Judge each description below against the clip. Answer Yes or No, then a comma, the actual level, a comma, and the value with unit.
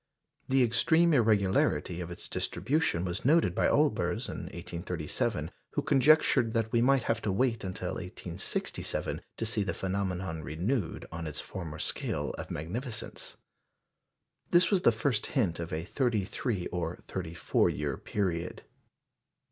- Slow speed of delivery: No, average, 145 wpm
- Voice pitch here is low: Yes, low, 100 Hz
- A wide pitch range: Yes, wide, 5.8 semitones